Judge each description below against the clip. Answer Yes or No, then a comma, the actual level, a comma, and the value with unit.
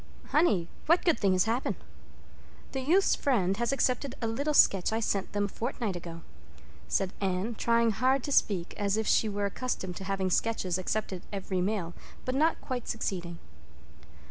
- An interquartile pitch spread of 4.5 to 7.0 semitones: Yes, average, 5.1 semitones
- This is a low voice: No, high, 210 Hz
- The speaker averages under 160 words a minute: No, average, 170 wpm